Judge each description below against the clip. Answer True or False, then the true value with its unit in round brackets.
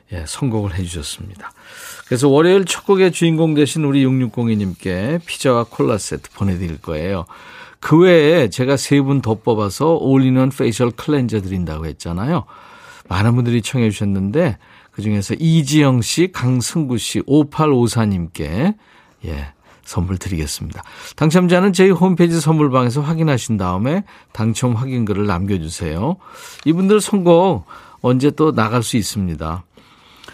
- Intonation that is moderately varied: False (7.5 semitones)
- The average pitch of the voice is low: True (125 Hz)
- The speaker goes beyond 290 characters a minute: True (300 characters per minute)